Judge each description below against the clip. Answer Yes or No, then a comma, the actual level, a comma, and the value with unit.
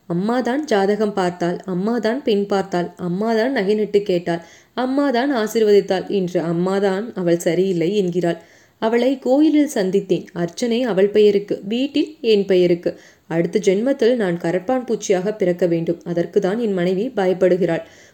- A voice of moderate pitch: No, high, 200 Hz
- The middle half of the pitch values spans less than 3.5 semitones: No, average, 3.9 semitones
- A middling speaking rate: Yes, average, 120 wpm